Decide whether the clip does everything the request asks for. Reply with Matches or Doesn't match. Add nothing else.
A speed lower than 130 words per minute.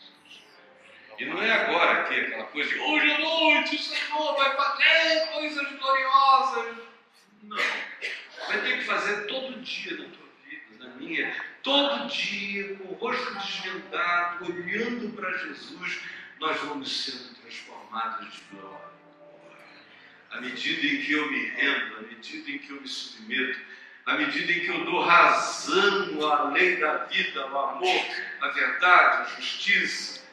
Doesn't match